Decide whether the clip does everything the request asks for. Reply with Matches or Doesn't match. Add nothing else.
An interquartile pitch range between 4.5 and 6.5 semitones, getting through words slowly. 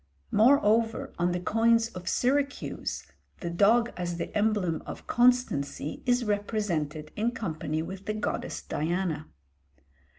Matches